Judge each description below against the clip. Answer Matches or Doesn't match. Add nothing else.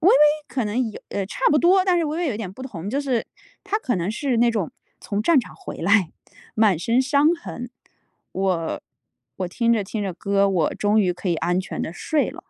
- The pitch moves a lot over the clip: Matches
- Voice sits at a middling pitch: Doesn't match